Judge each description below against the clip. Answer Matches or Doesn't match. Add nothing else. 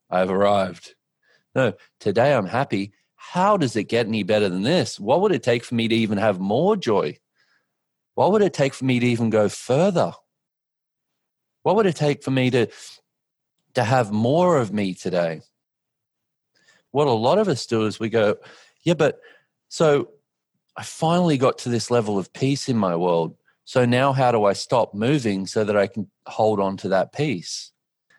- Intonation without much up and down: Doesn't match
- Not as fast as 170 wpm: Doesn't match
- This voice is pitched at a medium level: Doesn't match